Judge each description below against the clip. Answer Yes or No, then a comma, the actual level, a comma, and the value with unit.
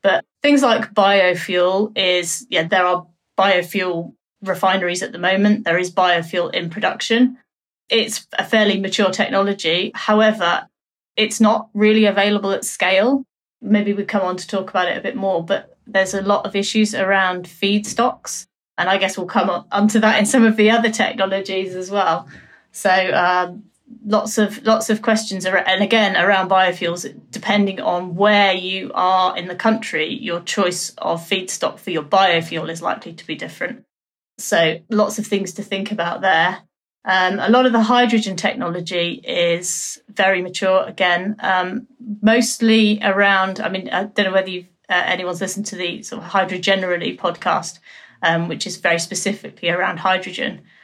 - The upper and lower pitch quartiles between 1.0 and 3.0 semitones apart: Yes, average, 2.7 semitones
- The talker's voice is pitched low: No, high, 195 Hz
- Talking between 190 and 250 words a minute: No, average, 170 wpm